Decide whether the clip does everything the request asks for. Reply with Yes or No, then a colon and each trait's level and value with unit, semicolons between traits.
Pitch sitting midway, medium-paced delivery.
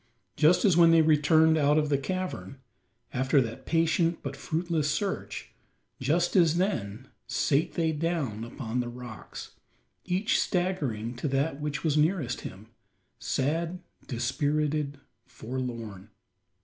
No: medium, 150 Hz; slow, 125 wpm